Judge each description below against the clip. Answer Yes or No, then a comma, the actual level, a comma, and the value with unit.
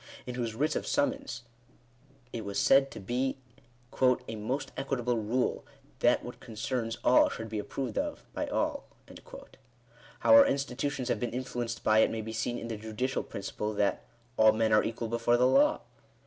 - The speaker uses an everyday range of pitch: Yes, average, 3.0 semitones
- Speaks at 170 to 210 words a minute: Yes, average, 180 wpm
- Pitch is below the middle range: Yes, low, 120 Hz